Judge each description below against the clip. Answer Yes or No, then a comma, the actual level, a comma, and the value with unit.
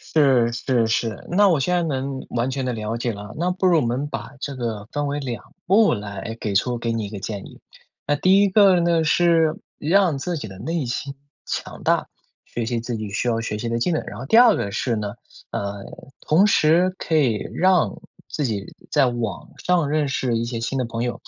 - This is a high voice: No, low, 130 Hz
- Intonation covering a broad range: Yes, wide, 6.2 semitones